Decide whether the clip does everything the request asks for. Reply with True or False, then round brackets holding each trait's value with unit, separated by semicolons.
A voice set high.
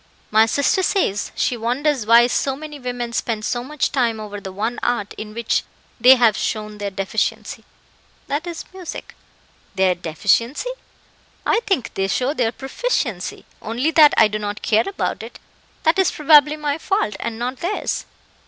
True (240 Hz)